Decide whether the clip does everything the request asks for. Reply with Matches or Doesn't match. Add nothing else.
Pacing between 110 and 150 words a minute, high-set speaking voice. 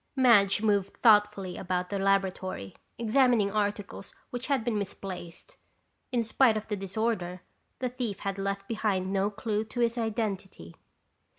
Matches